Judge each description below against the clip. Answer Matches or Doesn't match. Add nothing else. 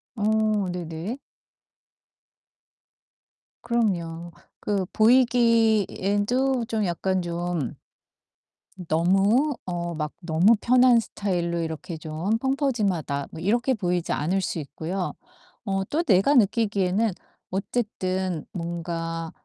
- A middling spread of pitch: Matches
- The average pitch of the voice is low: Doesn't match